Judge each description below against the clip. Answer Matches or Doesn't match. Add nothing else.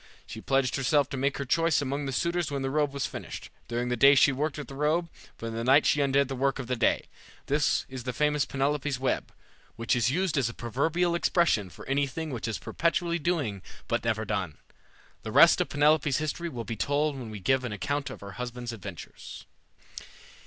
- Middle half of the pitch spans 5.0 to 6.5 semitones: Doesn't match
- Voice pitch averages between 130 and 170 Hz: Matches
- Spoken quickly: Matches